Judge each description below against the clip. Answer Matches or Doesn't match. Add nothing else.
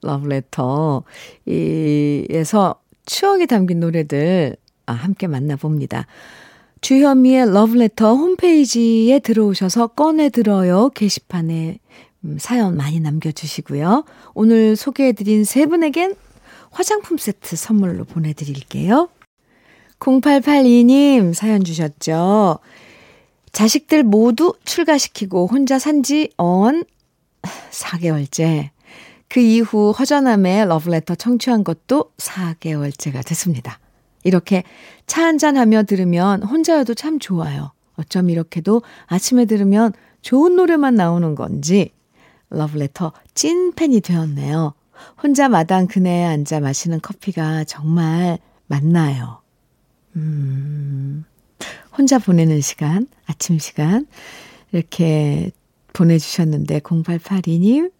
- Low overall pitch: Doesn't match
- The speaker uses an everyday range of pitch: Doesn't match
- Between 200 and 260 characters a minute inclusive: Matches